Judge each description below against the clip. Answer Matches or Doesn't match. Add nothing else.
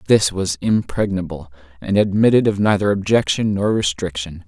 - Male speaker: Matches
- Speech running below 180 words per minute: Matches